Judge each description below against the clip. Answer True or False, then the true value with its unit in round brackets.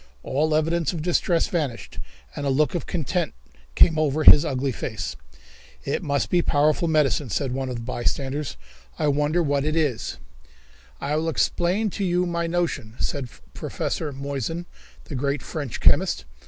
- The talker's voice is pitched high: False (150 Hz)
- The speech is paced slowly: False (165 wpm)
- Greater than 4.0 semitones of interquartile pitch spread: False (3.4 semitones)